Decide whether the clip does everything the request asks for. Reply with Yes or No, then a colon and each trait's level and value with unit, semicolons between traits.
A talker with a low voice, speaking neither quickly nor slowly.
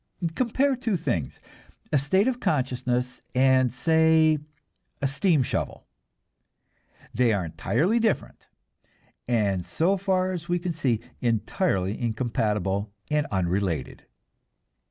No: low, 130 Hz; slow, 115 wpm